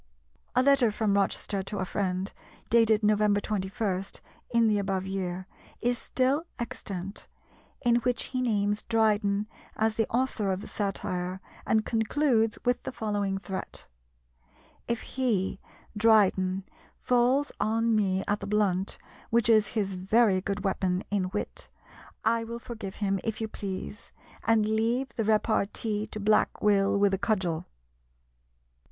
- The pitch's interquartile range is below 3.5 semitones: Yes, average, 2.7 semitones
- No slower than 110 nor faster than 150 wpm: Yes, average, 140 wpm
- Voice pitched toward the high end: Yes, high, 210 Hz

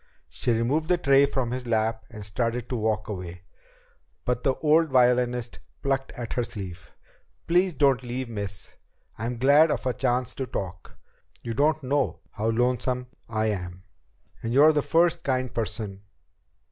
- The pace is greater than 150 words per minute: Yes, average, 160 wpm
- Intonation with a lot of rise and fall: No, average, 3.6 semitones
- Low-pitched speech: Yes, low, 125 Hz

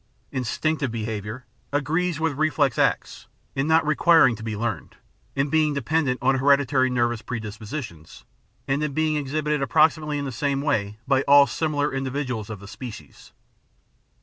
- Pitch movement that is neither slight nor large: Yes, average, 4.2 semitones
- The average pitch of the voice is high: No, low, 135 Hz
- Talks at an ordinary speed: Yes, average, 155 wpm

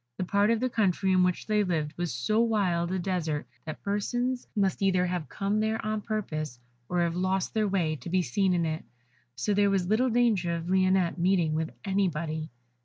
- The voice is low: No, medium, 185 Hz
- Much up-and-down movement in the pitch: No, average, 3.4 semitones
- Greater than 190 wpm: Yes, average, 200 wpm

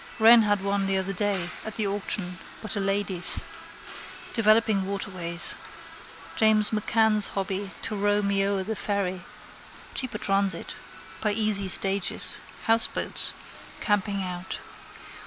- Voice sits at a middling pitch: No, high, 200 Hz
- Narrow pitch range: Yes, narrow, 1.7 semitones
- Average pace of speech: No, slow, 120 wpm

